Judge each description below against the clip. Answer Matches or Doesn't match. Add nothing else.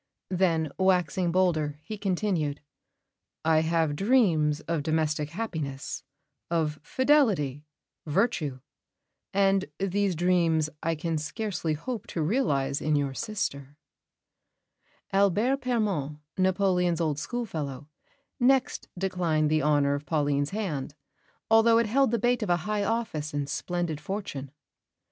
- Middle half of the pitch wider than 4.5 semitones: Matches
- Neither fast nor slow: Doesn't match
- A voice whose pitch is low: Doesn't match